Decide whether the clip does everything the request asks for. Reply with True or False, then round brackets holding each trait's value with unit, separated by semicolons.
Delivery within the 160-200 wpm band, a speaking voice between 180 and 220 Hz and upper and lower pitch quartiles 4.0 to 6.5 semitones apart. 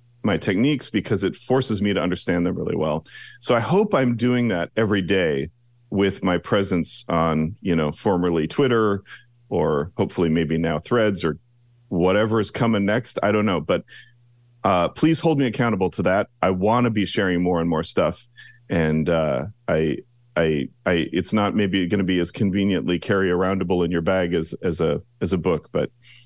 False (185 wpm; 100 Hz; 5.6 semitones)